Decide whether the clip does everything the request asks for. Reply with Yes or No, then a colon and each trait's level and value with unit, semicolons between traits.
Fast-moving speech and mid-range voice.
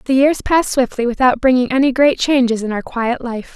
No: fast, 220 wpm; very high, 255 Hz